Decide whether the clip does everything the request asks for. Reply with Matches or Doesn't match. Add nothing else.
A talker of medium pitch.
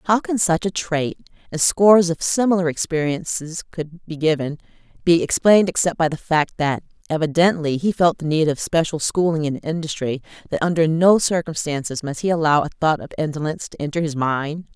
Matches